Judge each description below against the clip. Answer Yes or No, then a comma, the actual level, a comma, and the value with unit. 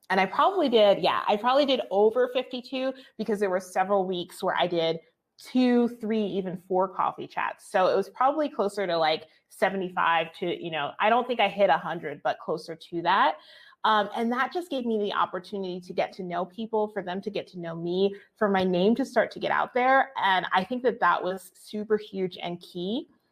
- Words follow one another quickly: Yes, fast, 225 wpm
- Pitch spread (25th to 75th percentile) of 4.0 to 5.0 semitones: Yes, average, 4.5 semitones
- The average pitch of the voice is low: No, high, 200 Hz